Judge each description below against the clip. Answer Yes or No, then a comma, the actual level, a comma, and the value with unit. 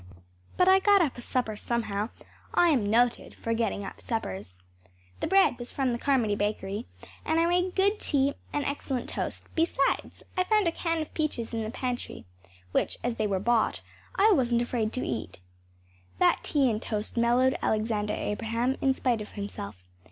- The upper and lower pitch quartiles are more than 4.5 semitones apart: Yes, average, 5.2 semitones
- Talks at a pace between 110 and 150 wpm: No, average, 180 wpm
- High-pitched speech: Yes, high, 240 Hz